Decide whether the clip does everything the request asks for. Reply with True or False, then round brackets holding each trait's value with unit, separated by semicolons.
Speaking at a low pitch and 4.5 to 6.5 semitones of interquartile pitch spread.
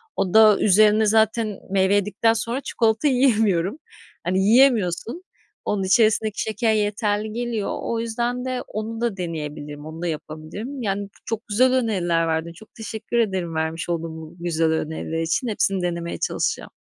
False (205 Hz; 4.9 semitones)